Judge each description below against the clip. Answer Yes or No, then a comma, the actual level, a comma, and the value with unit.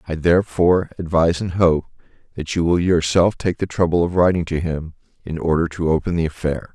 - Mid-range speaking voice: No, very low, 85 Hz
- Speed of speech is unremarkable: Yes, average, 195 wpm